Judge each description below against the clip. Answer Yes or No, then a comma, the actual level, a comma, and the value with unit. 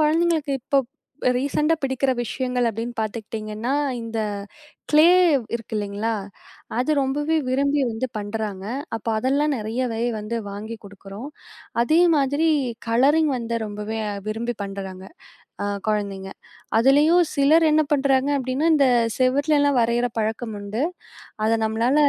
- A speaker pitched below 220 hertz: No, high, 240 Hz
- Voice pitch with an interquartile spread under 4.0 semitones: No, average, 4.5 semitones